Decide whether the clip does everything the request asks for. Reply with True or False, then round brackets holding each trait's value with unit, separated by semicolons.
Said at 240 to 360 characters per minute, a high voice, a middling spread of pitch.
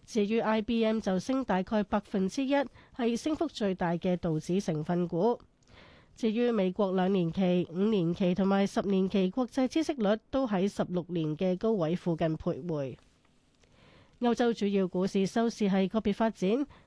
True (245 characters per minute; 195 Hz; 3.9 semitones)